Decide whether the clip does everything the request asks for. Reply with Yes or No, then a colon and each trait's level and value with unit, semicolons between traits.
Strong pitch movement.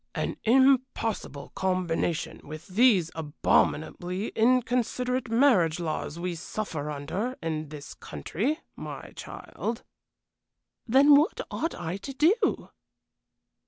Yes: wide, 7.8 semitones